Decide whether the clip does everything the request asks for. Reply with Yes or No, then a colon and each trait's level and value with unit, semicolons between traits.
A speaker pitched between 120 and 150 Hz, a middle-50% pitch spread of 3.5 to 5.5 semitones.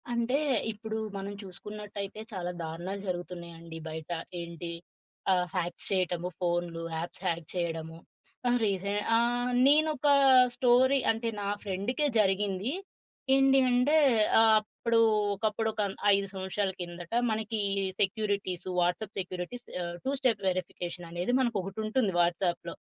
No: high, 195 Hz; average, 4.3 semitones